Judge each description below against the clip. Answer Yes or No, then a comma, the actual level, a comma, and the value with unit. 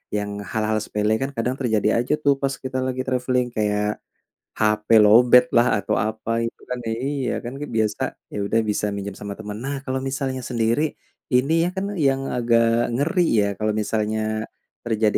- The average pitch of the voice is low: Yes, low, 115 Hz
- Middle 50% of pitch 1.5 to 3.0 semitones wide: No, average, 3.4 semitones